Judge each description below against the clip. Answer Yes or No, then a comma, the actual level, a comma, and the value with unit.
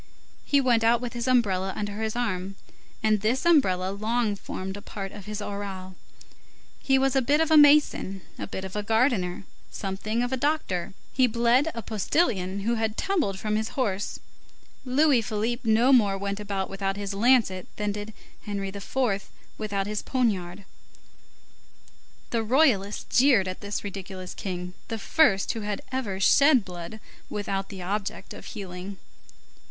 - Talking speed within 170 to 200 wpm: No, average, 160 wpm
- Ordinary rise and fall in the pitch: Yes, average, 3.9 semitones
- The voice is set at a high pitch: Yes, high, 210 Hz